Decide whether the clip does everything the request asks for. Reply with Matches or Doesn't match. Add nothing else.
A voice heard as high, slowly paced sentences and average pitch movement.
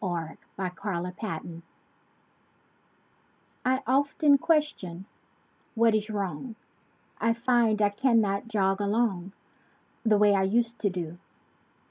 Matches